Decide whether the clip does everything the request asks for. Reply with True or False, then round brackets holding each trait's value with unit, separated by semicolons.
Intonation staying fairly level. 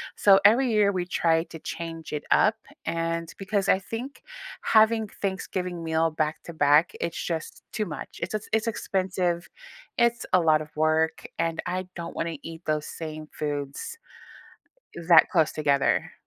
False (3.6 semitones)